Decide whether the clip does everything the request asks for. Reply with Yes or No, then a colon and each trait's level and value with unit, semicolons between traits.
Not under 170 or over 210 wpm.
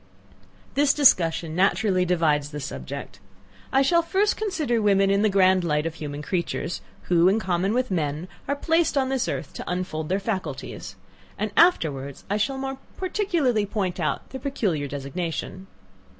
No: average, 160 wpm